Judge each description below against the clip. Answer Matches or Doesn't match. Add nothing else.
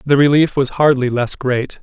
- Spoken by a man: Matches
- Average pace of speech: Matches